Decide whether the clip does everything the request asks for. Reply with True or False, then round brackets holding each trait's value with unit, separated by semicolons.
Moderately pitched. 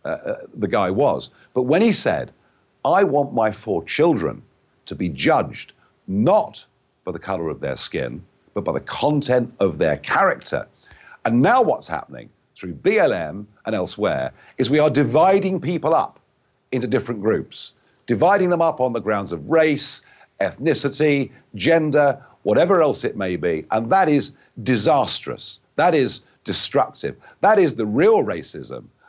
True (145 Hz)